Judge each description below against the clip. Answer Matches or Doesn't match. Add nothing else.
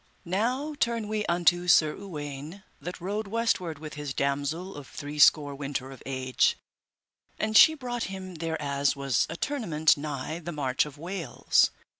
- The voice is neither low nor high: Matches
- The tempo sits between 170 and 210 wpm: Doesn't match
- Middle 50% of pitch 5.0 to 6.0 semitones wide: Matches